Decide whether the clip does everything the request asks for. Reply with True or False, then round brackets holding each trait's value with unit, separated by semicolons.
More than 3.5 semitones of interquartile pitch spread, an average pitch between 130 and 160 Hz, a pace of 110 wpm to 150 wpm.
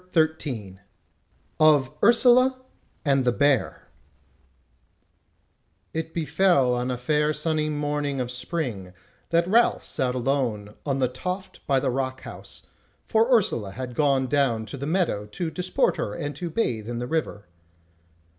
True (4.6 semitones; 140 Hz; 140 wpm)